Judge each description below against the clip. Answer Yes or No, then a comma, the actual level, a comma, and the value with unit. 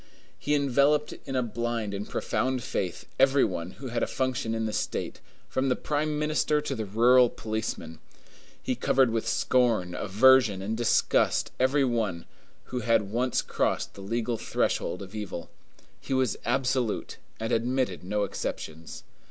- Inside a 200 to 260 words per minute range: No, average, 155 wpm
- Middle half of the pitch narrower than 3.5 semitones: No, average, 3.8 semitones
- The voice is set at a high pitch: No, low, 120 Hz